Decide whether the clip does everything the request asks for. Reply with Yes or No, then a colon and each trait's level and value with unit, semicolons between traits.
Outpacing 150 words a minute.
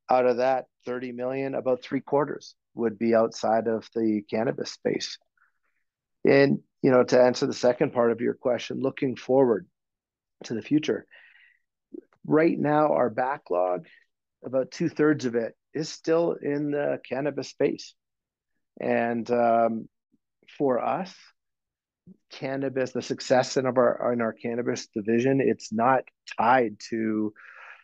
No: slow, 135 wpm